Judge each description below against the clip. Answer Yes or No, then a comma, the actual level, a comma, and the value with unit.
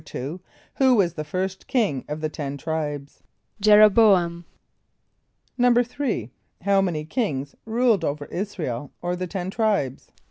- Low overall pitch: No, medium, 180 Hz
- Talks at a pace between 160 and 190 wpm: No, average, 145 wpm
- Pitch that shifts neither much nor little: No, wide, 6.0 semitones